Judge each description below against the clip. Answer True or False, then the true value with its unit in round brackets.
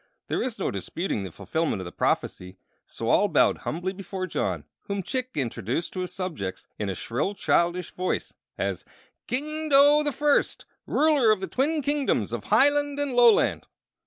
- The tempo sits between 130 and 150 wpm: False (170 wpm)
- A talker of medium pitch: False (195 Hz)